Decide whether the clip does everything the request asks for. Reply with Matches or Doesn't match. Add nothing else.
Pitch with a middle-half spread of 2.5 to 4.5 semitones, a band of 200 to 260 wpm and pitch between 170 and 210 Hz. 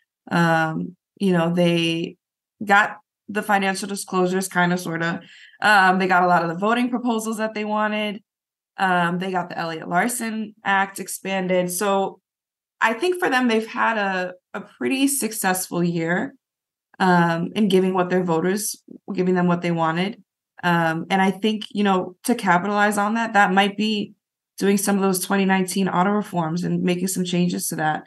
Doesn't match